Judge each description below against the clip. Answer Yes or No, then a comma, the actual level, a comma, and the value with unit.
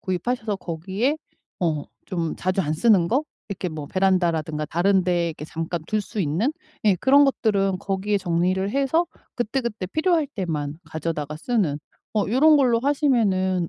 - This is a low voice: No, high, 190 Hz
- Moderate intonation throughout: No, wide, 5.9 semitones